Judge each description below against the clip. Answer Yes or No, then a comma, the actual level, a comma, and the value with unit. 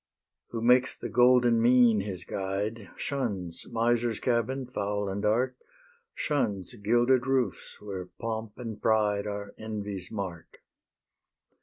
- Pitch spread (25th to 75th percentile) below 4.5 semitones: Yes, average, 3.1 semitones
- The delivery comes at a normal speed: No, slow, 120 wpm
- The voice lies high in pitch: No, low, 110 Hz